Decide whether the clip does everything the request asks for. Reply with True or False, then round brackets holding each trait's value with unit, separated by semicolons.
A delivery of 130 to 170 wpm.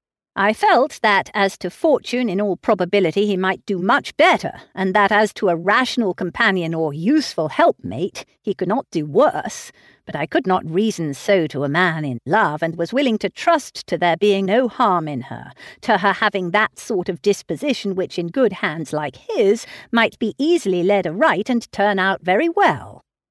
False (195 wpm)